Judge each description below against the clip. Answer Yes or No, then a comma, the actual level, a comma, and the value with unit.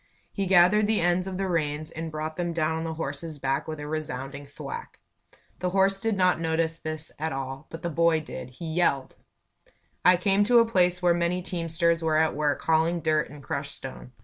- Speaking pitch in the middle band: Yes, medium, 165 Hz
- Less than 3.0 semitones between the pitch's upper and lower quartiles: Yes, narrow, 2.6 semitones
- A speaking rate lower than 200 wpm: No, fast, 205 wpm